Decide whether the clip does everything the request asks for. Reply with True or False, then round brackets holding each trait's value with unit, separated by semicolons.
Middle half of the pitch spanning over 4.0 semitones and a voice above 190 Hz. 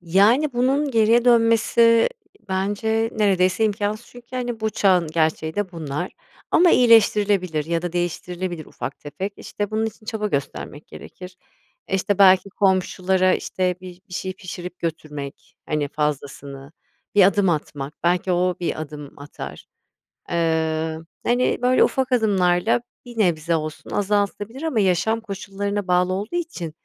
False (4.7 semitones; 185 Hz)